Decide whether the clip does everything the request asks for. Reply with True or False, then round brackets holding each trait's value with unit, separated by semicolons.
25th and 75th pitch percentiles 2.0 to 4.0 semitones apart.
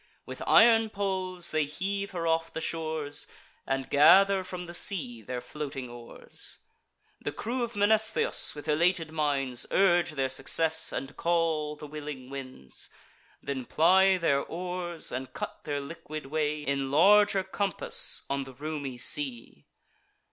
False (4.8 semitones)